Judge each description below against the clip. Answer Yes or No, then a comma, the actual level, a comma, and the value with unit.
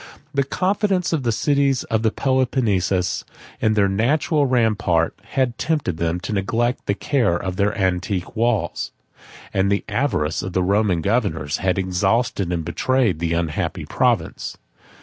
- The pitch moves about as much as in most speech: No, wide, 6.1 semitones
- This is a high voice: No, low, 105 Hz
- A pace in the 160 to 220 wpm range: No, average, 145 wpm